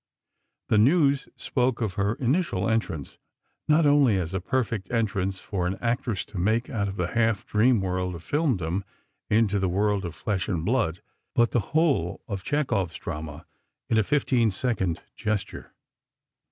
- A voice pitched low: Yes, low, 105 Hz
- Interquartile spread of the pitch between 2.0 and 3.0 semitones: No, average, 4.7 semitones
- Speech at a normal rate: Yes, average, 160 wpm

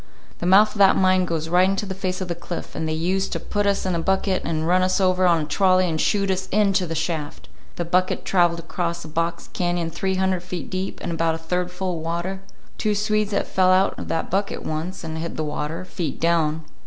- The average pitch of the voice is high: No, medium, 180 Hz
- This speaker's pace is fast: Yes, fast, 240 wpm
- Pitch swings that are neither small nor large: No, narrow, 2.3 semitones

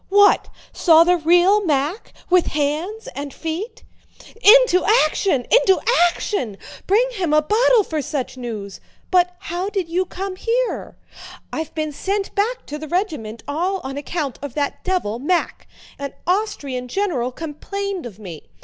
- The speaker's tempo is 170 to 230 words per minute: No, average, 150 wpm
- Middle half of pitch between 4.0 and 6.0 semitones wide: Yes, wide, 5.6 semitones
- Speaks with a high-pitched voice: Yes, very high, 345 Hz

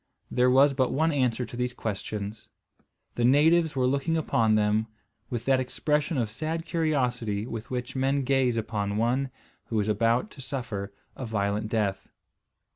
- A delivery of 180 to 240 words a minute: No, average, 160 wpm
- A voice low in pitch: Yes, low, 125 Hz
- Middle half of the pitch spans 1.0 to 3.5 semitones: No, average, 3.9 semitones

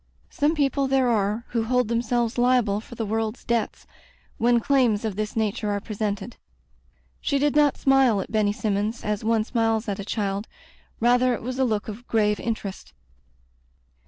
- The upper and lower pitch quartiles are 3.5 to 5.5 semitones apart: No, average, 2.8 semitones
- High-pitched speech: Yes, high, 225 Hz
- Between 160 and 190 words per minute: Yes, average, 170 wpm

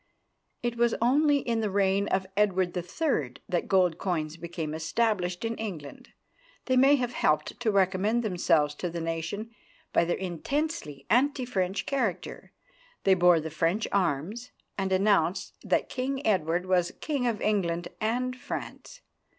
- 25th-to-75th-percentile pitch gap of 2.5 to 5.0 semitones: No, wide, 5.5 semitones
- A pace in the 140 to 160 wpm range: Yes, average, 150 wpm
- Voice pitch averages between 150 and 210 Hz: Yes, high, 190 Hz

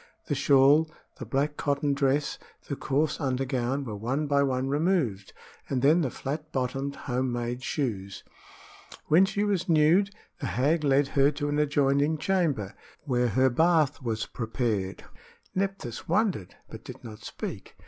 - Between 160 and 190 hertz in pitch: No, medium, 140 Hz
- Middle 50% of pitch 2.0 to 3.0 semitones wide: No, average, 3.4 semitones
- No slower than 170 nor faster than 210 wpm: No, average, 150 wpm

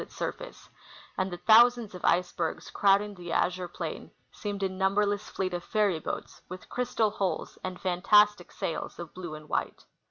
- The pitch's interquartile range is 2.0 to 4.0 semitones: Yes, average, 2.7 semitones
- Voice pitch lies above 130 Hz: Yes, high, 190 Hz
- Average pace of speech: Yes, average, 170 wpm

